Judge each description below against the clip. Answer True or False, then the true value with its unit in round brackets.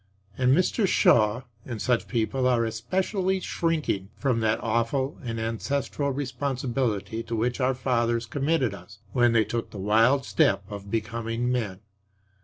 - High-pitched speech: False (120 Hz)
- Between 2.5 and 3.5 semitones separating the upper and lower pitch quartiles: True (3.0 semitones)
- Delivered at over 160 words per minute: False (145 wpm)